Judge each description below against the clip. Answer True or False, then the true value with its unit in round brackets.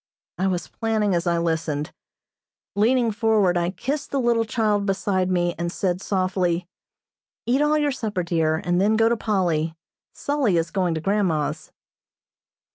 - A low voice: False (190 Hz)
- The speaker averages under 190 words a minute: True (155 wpm)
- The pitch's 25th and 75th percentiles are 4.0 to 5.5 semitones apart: True (4.4 semitones)